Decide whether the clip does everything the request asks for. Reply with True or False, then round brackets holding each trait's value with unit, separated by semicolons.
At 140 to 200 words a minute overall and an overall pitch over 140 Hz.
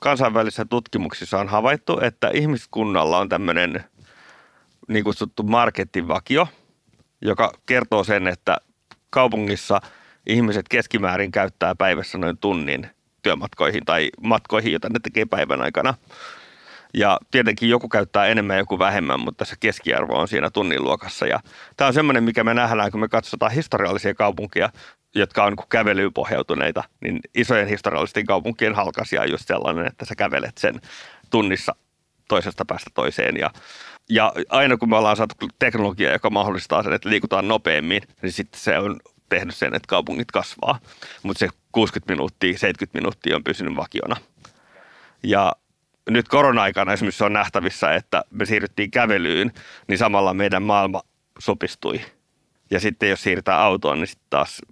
False (145 wpm; 105 Hz)